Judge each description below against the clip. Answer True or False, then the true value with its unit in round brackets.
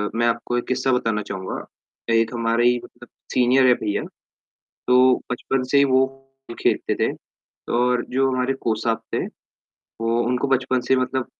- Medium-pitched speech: False (125 Hz)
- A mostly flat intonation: True (1.9 semitones)